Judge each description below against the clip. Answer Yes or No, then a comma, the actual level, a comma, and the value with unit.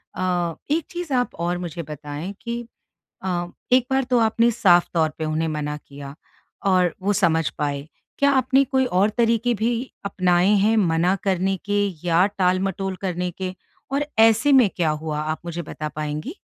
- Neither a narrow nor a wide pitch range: No, wide, 5.7 semitones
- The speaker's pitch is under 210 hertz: Yes, medium, 185 Hz